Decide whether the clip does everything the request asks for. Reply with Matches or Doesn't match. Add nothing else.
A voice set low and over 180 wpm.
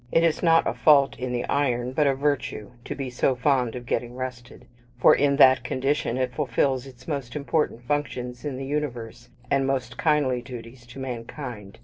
Matches